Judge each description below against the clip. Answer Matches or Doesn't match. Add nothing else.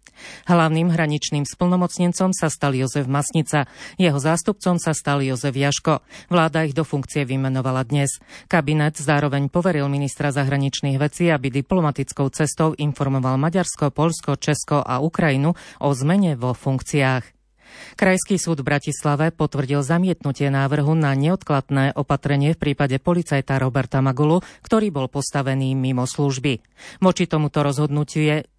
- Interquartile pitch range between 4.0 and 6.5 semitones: Doesn't match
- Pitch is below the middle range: Doesn't match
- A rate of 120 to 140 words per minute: Matches